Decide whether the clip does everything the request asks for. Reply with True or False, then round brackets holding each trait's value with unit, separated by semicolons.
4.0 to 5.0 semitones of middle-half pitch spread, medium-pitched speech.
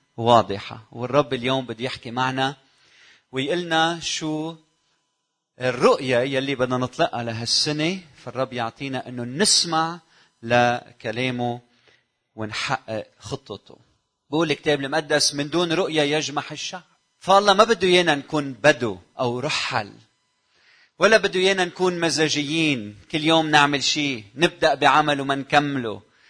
True (4.6 semitones; 145 Hz)